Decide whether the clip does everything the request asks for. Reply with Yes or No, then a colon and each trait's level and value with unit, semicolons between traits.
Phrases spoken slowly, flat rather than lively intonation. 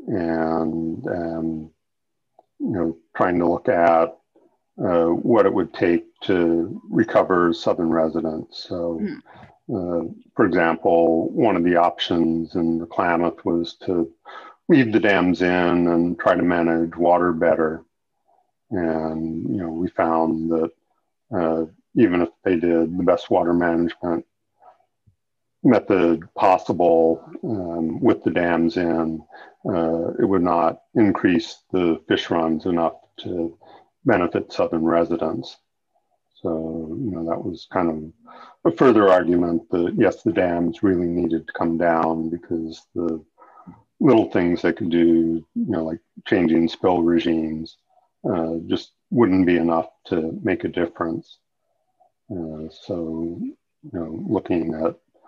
Yes: slow, 130 wpm; narrow, 0.9 semitones